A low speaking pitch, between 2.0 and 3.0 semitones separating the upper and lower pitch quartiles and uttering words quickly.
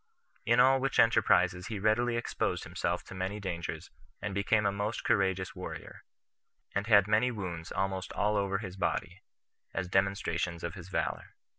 No: low, 100 Hz; narrow, 2.5 semitones; average, 160 wpm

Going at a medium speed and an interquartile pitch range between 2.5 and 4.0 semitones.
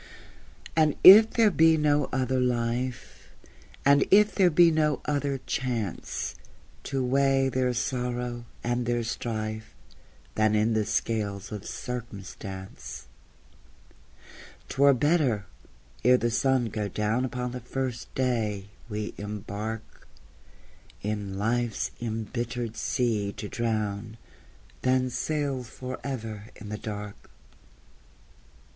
No: slow, 110 wpm; average, 3.6 semitones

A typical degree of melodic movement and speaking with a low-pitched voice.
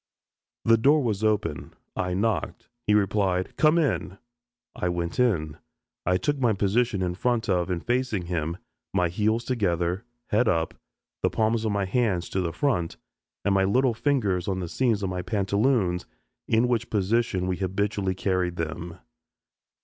Yes: average, 4.2 semitones; low, 100 Hz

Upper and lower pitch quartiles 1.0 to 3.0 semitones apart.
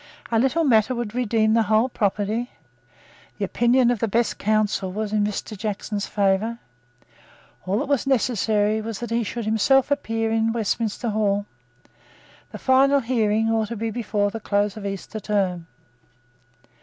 Yes: narrow, 2.4 semitones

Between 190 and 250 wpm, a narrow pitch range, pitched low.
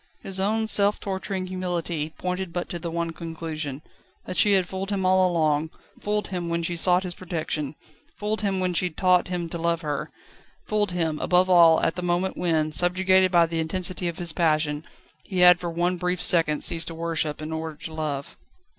No: average, 200 wpm; narrow, 2.3 semitones; medium, 175 Hz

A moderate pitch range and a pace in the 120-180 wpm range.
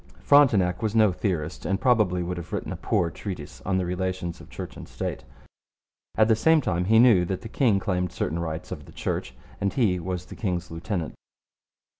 No: average, 3.8 semitones; average, 200 wpm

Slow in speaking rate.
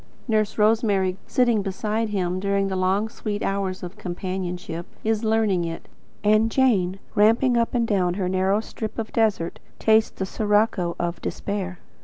No: average, 150 wpm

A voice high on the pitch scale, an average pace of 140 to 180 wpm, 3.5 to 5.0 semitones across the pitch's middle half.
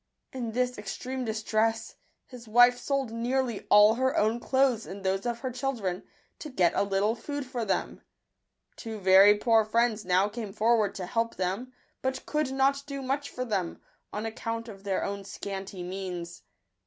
Yes: high, 225 Hz; average, 170 wpm; average, 4.1 semitones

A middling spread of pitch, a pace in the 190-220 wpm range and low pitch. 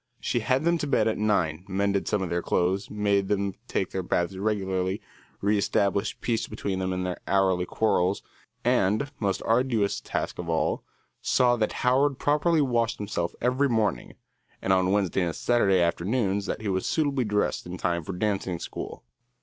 No: average, 3.6 semitones; average, 175 wpm; low, 100 Hz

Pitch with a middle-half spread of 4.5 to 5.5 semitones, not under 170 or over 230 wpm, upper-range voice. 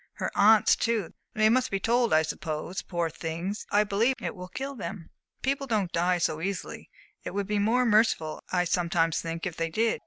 Yes: average, 4.9 semitones; average, 195 wpm; high, 195 Hz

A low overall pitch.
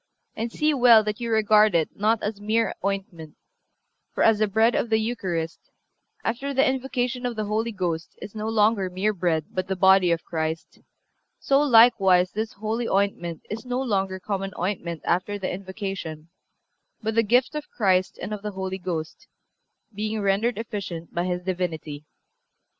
No: high, 205 Hz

